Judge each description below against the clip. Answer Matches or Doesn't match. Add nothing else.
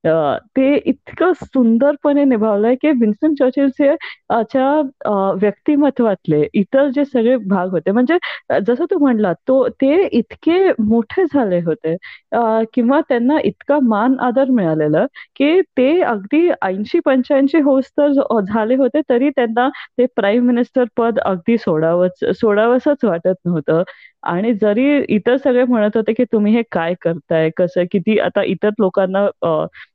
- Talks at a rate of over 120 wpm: Matches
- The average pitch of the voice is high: Matches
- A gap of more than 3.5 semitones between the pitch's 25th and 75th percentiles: Matches